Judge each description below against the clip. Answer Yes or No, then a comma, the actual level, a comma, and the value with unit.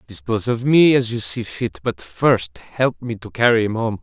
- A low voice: Yes, low, 120 Hz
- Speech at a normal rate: No, fast, 225 wpm